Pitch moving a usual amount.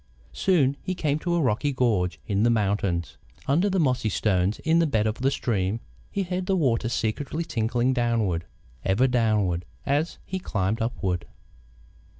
No: wide, 6.1 semitones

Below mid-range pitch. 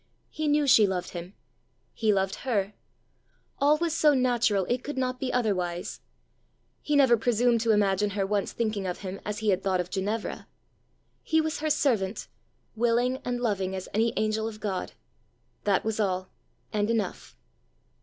No: high, 215 Hz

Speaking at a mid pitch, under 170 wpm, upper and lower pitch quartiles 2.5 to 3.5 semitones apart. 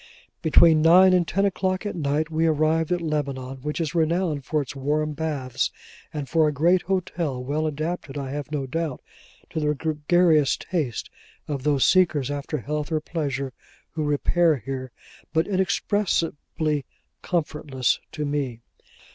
Yes: medium, 155 Hz; average, 150 wpm; average, 2.8 semitones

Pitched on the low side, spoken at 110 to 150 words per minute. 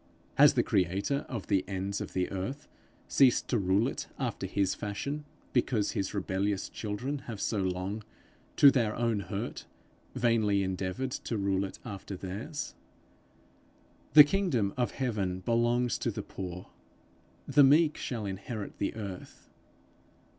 Yes: low, 105 Hz; average, 140 wpm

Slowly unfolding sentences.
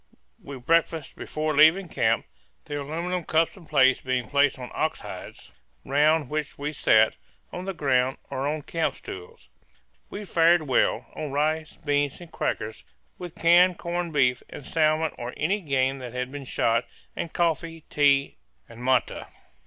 No: average, 160 wpm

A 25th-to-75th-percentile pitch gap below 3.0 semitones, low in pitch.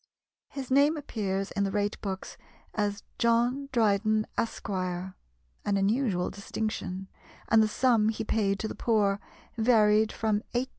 No: narrow, 2.6 semitones; high, 215 Hz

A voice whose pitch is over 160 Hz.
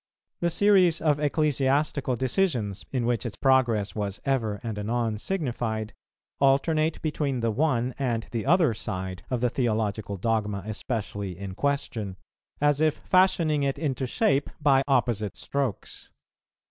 No: low, 125 Hz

